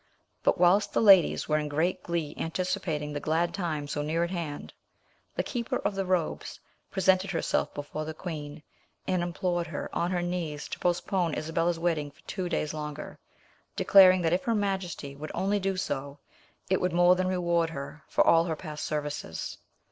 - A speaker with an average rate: Yes, average, 180 wpm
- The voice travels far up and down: No, average, 3.3 semitones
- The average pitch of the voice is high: No, medium, 170 Hz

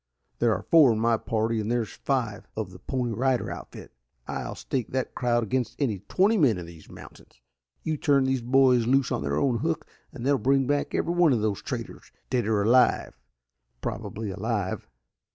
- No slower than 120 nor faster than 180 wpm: No, average, 190 wpm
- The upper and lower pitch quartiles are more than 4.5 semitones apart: No, average, 3.7 semitones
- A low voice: Yes, low, 120 Hz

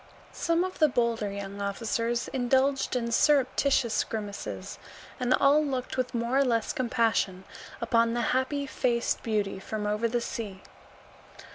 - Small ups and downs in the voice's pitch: No, average, 3.5 semitones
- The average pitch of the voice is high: Yes, high, 235 Hz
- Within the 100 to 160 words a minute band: Yes, average, 140 wpm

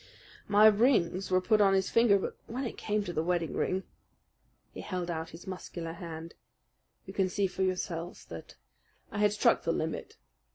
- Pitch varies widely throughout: No, average, 3.2 semitones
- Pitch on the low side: No, medium, 185 Hz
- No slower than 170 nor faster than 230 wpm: Yes, average, 180 wpm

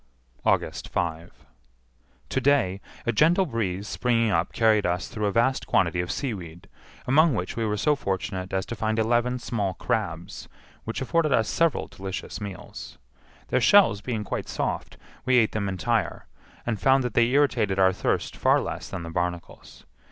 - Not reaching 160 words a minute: No, average, 165 wpm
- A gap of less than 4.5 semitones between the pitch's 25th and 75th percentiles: No, average, 4.8 semitones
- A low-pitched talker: Yes, low, 110 Hz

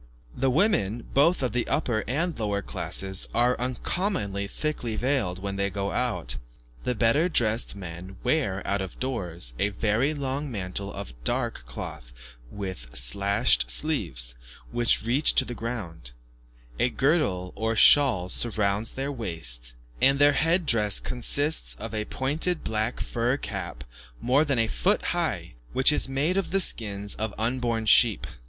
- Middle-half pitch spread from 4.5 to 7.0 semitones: Yes, wide, 5.4 semitones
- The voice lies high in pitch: No, low, 115 Hz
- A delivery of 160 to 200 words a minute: No, average, 150 wpm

